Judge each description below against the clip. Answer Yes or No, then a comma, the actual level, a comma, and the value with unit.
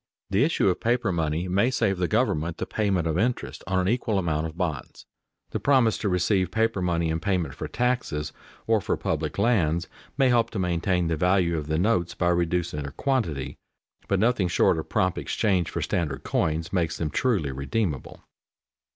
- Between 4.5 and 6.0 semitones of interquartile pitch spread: Yes, average, 5.1 semitones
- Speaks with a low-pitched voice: Yes, very low, 90 Hz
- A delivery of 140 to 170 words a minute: No, average, 185 wpm